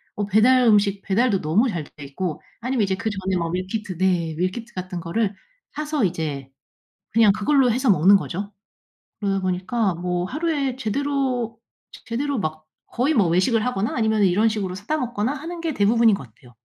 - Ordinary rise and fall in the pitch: Yes, average, 4.9 semitones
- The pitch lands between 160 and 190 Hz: No, high, 205 Hz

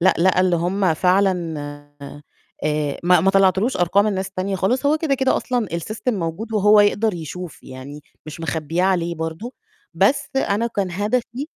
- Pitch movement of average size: Yes, average, 4.1 semitones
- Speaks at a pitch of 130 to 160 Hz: No, high, 190 Hz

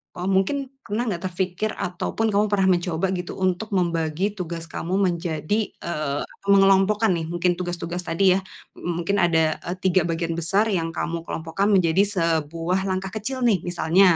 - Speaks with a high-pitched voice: No, medium, 175 Hz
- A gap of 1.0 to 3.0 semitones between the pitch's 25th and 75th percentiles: Yes, narrow, 2.6 semitones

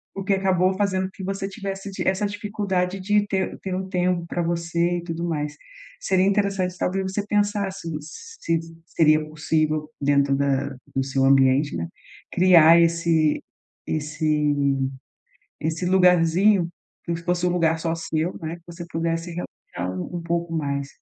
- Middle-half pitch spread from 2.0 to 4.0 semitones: Yes, average, 3.4 semitones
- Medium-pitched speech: Yes, medium, 170 Hz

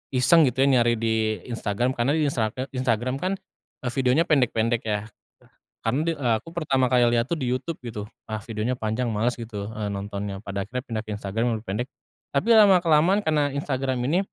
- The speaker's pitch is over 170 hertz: No, low, 125 Hz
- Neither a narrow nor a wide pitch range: Yes, average, 4.2 semitones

